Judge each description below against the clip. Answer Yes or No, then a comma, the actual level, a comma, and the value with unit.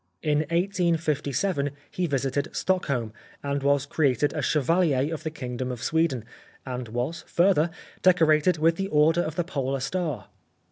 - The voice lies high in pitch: No, medium, 150 Hz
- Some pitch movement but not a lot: Yes, average, 3.8 semitones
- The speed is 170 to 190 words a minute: No, average, 145 wpm